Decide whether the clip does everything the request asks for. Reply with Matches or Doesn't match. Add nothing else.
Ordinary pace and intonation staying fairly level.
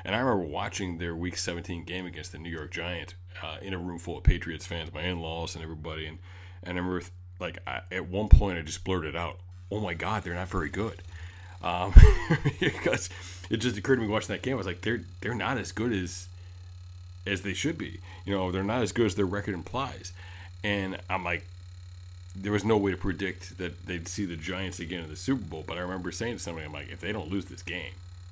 Doesn't match